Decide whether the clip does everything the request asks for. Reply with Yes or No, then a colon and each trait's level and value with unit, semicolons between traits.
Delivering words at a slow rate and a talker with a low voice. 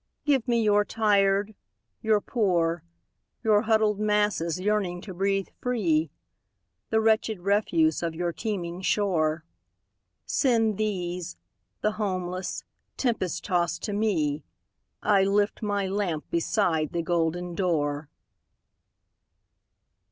No: slow, 95 wpm; high, 195 Hz